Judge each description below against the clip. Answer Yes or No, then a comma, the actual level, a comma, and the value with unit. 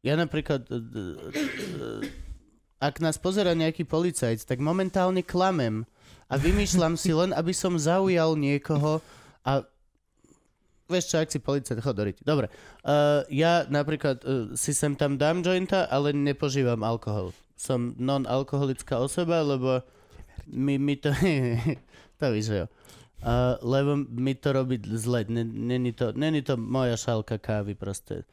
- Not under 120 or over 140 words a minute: Yes, average, 125 wpm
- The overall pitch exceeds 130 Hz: Yes, medium, 140 Hz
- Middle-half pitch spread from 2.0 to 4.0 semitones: No, average, 4.6 semitones